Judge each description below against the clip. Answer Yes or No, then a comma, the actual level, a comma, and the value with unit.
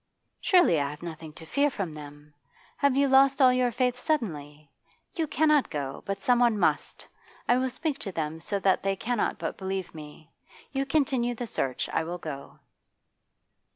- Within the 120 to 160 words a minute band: No, average, 175 wpm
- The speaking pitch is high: Yes, high, 200 Hz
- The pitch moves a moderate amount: No, wide, 8.9 semitones